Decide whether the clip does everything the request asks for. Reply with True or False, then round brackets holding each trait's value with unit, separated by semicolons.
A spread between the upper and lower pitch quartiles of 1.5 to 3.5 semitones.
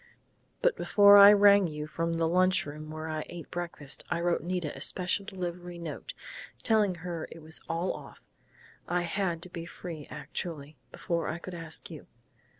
True (2.4 semitones)